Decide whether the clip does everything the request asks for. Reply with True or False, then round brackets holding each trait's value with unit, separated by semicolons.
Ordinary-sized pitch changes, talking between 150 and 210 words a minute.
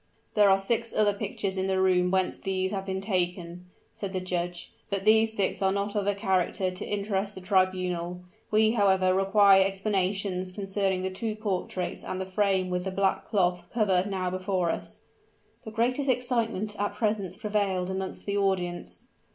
False (1.8 semitones; 175 wpm)